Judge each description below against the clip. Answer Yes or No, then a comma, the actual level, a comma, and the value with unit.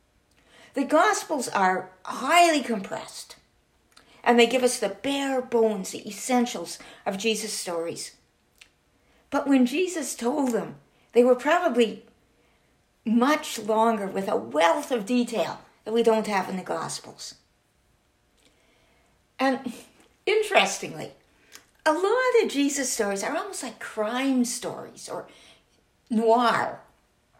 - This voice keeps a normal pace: No, slow, 115 wpm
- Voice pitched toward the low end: No, high, 240 Hz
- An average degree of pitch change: Yes, average, 4.4 semitones